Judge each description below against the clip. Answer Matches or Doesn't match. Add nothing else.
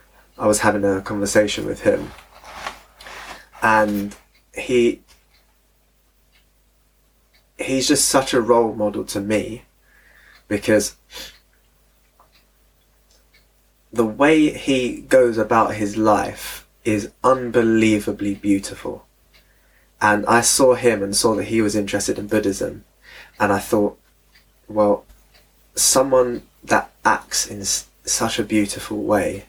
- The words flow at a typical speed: Doesn't match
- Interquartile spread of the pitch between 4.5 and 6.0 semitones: Doesn't match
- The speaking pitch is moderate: Doesn't match